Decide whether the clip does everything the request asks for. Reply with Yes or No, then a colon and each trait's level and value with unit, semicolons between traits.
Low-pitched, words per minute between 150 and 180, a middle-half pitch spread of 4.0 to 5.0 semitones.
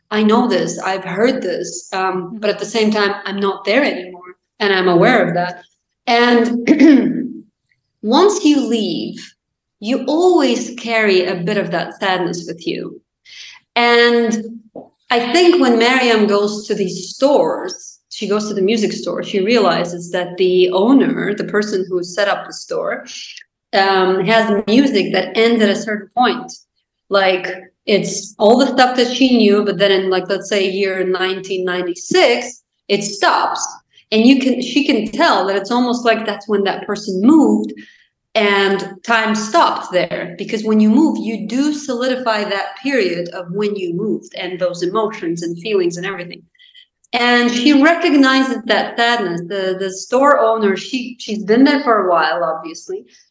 No: high, 210 Hz; average, 165 wpm; average, 4.5 semitones